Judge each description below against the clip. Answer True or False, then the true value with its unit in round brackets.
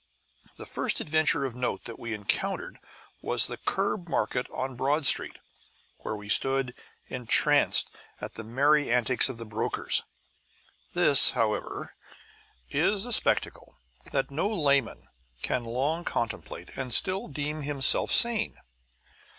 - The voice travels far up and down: False (4.2 semitones)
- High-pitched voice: False (135 Hz)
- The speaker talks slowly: True (130 wpm)